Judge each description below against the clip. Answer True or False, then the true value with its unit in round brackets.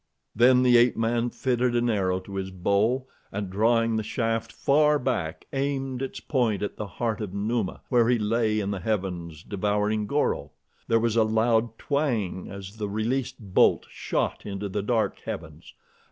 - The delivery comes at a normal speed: True (170 wpm)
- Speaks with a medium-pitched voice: False (110 Hz)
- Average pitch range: True (3.2 semitones)